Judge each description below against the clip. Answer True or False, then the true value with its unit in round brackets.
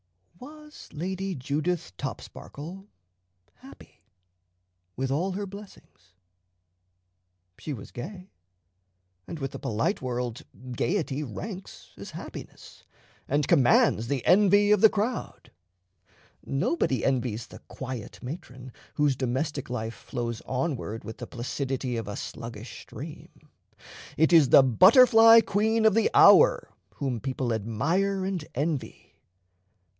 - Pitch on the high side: False (140 Hz)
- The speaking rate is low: True (115 wpm)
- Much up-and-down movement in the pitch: True (7.7 semitones)